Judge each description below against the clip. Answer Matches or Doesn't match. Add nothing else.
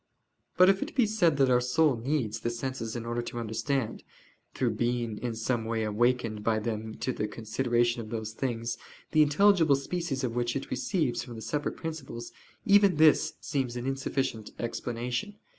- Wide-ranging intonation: Doesn't match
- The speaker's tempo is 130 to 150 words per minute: Doesn't match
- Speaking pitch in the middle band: Doesn't match